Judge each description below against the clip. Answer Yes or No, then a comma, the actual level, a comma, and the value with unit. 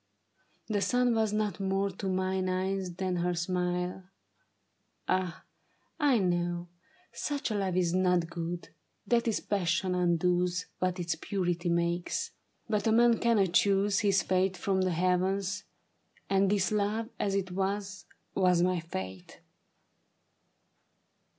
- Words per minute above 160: No, slow, 135 wpm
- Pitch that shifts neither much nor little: No, narrow, 2.1 semitones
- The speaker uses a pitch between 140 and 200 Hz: Yes, medium, 185 Hz